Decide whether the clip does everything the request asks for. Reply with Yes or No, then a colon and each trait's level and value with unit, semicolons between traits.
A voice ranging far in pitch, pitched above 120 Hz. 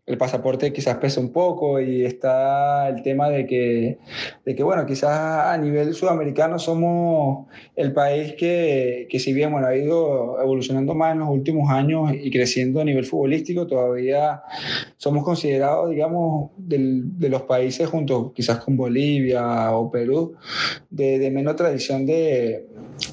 No: average, 3.1 semitones; medium, 140 Hz